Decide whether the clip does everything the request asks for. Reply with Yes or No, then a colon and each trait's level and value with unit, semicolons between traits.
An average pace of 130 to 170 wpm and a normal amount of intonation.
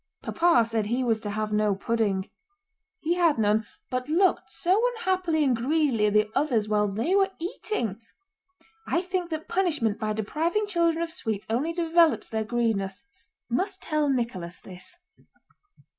No: average, 155 wpm; wide, 7.8 semitones